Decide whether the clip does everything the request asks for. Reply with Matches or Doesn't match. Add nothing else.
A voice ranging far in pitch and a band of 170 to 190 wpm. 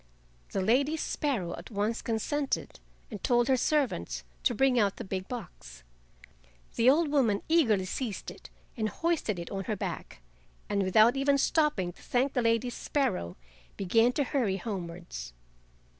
Doesn't match